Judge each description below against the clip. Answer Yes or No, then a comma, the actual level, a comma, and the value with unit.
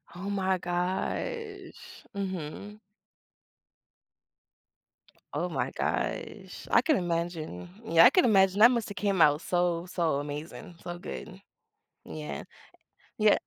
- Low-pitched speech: No, medium, 180 Hz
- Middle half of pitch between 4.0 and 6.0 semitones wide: No, average, 3.5 semitones